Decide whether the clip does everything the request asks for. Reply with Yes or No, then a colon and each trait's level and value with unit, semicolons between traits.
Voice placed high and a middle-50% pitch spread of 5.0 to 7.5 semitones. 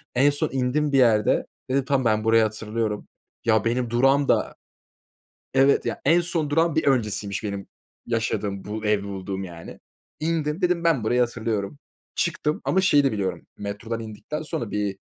No: low, 115 Hz; wide, 5.5 semitones